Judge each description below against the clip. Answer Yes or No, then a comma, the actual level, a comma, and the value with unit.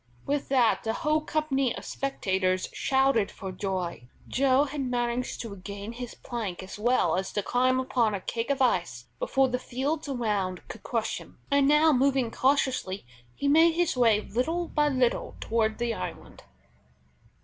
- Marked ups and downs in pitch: No, average, 4.8 semitones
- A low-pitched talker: No, high, 245 Hz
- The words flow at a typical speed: Yes, average, 165 wpm